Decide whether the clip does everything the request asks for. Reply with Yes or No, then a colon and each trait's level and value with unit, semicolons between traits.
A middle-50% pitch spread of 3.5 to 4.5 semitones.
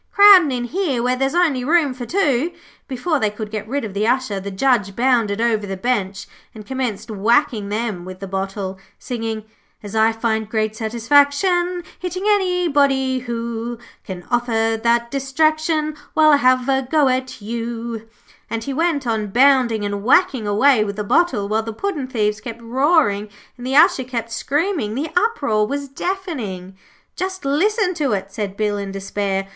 No: average, 5.1 semitones